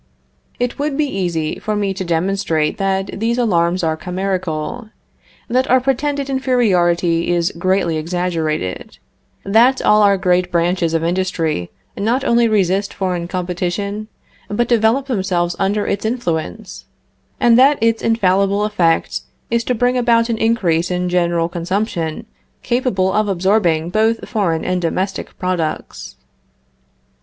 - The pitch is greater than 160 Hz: Yes, high, 190 Hz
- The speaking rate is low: Yes, slow, 130 wpm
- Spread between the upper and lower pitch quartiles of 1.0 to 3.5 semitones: No, average, 4.7 semitones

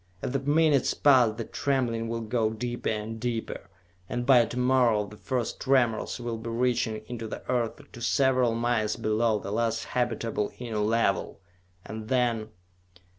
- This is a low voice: Yes, low, 115 Hz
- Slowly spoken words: No, average, 160 wpm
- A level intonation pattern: Yes, narrow, 2.0 semitones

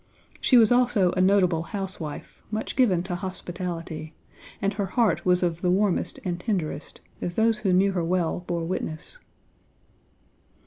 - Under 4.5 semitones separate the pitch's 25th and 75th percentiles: Yes, average, 2.8 semitones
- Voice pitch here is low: No, medium, 185 Hz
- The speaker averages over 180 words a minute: No, average, 150 wpm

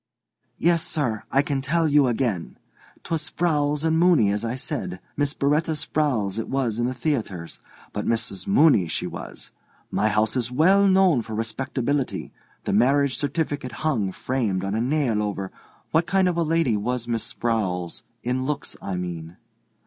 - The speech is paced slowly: No, average, 165 wpm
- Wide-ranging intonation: Yes, wide, 5.7 semitones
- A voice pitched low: Yes, low, 130 Hz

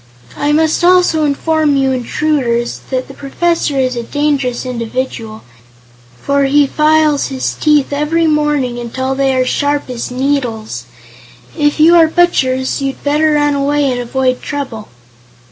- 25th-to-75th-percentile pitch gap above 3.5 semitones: No, average, 2.8 semitones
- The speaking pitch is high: Yes, very high, 280 Hz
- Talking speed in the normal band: Yes, average, 145 wpm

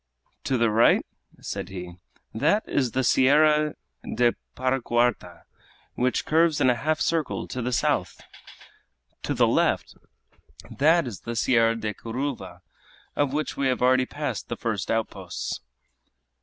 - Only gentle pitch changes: No, average, 4.0 semitones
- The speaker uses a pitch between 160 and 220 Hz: No, low, 125 Hz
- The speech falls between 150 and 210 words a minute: No, average, 140 wpm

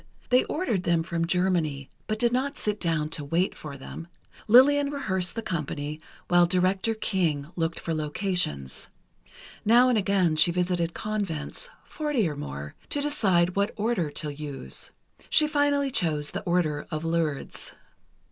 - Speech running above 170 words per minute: No, average, 150 wpm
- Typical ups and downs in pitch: No, wide, 5.9 semitones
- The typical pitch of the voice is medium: Yes, medium, 180 Hz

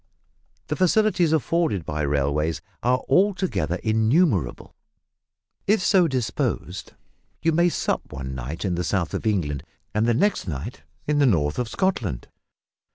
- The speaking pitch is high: No, low, 110 Hz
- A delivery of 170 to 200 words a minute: No, average, 140 wpm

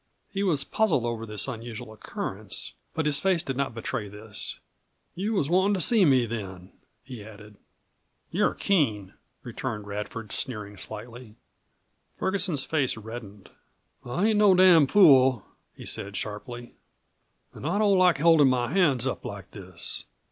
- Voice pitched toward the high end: No, low, 125 Hz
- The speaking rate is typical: Yes, average, 150 wpm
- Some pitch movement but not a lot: No, wide, 8.1 semitones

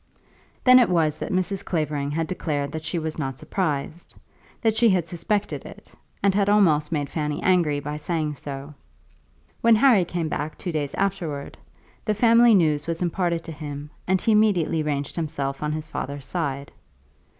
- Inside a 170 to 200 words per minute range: Yes, average, 175 wpm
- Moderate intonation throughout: Yes, average, 4.1 semitones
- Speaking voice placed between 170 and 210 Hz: No, medium, 160 Hz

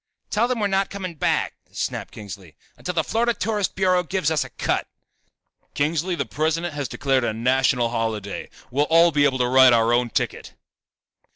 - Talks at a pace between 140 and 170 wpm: No, average, 180 wpm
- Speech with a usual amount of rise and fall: No, wide, 6.8 semitones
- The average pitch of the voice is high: No, medium, 150 Hz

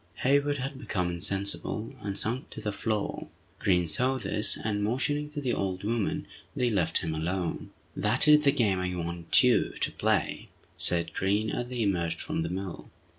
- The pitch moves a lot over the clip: Yes, wide, 5.7 semitones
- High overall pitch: No, low, 105 Hz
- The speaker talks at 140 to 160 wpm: No, average, 175 wpm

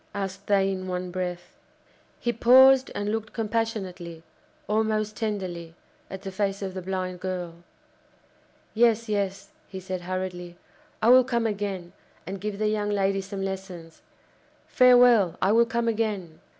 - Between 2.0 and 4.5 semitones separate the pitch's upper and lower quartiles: Yes, average, 2.9 semitones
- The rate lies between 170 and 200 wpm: No, average, 145 wpm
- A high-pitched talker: Yes, high, 195 Hz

